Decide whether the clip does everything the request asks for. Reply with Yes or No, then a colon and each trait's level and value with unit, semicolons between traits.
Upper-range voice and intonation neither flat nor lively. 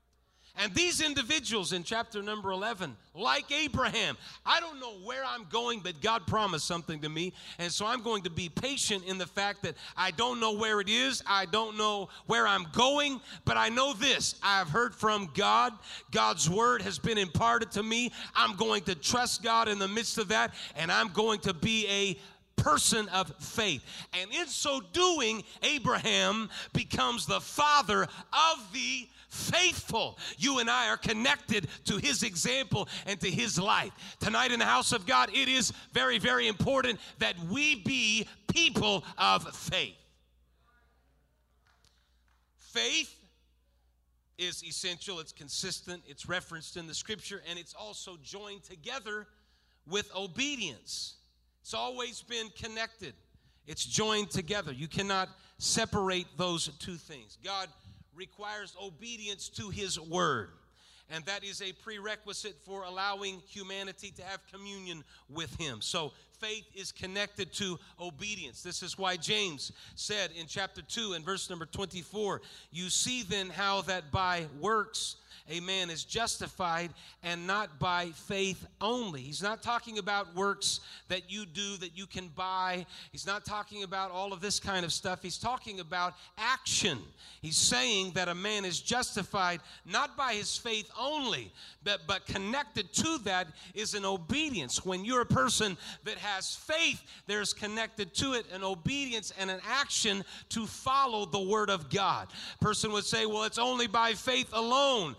Yes: high, 195 Hz; average, 3.9 semitones